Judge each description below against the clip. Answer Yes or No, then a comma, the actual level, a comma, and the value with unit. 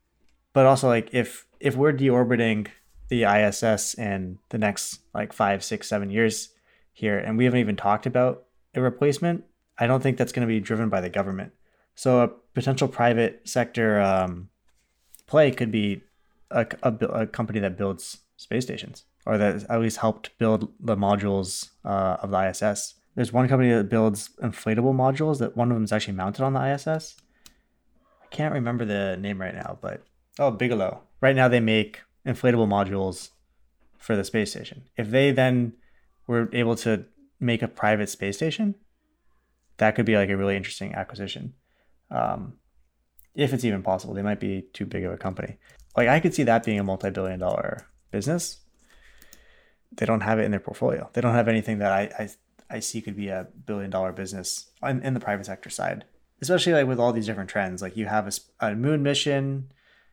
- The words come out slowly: No, average, 185 wpm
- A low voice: Yes, low, 110 Hz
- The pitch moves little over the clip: No, average, 4.2 semitones